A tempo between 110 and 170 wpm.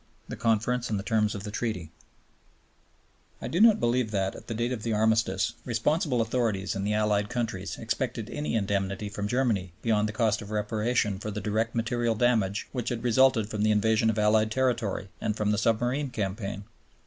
No: average, 190 wpm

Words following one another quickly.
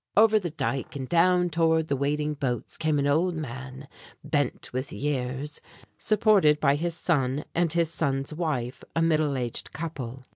No: average, 160 wpm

